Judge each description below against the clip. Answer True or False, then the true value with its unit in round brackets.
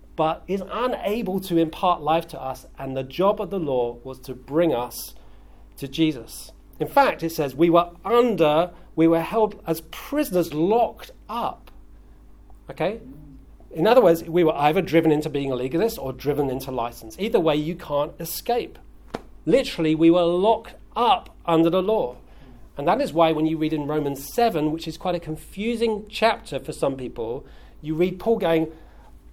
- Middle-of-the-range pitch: True (165 Hz)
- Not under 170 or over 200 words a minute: True (175 wpm)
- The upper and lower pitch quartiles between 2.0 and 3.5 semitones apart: False (4.2 semitones)